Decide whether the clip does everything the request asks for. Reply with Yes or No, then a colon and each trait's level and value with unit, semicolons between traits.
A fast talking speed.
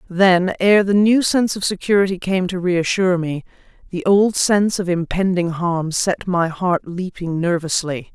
No: average, 160 wpm